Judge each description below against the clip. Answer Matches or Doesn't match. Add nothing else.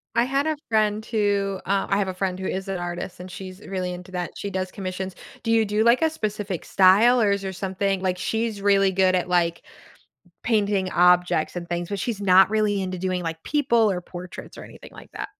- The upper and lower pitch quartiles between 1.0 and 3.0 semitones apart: Matches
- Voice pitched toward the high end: Matches